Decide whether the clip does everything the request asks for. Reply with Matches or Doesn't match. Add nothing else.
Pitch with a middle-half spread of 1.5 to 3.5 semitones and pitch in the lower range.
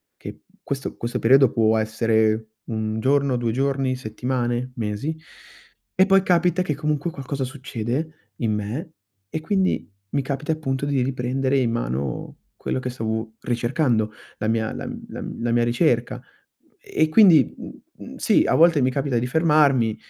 Doesn't match